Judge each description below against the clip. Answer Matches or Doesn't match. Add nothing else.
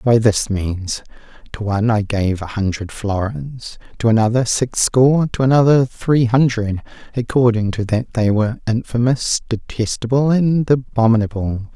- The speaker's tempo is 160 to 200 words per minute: Doesn't match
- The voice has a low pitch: Matches